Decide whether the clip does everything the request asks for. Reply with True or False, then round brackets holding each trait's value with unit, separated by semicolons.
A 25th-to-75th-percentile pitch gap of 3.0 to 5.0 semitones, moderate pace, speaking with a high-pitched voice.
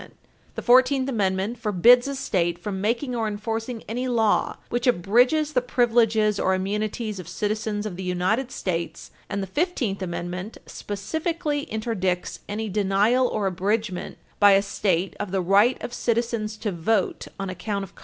True (3.9 semitones; 165 wpm; 215 Hz)